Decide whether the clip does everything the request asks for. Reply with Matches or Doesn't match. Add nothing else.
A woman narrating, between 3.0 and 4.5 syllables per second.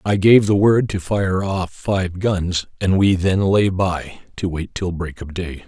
Doesn't match